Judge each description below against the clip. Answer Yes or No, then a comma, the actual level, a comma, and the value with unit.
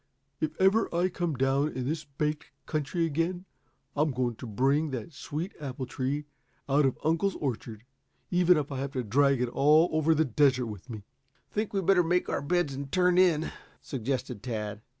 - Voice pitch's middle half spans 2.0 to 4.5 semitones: Yes, average, 4.2 semitones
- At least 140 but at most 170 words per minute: No, average, 185 wpm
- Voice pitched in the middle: Yes, medium, 145 Hz